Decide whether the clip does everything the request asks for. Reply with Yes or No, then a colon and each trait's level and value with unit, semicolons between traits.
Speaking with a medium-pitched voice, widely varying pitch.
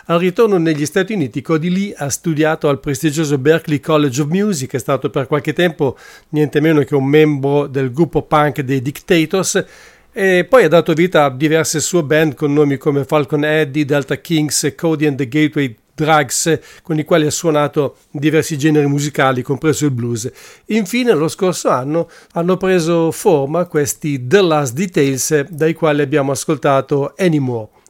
No: medium, 155 Hz; narrow, 2.5 semitones